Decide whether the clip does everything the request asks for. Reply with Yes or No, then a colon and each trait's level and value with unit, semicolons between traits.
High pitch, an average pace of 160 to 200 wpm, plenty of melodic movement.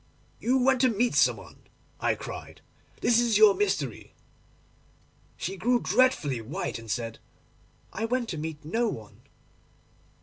No: high, 210 Hz; average, 140 wpm; wide, 8.5 semitones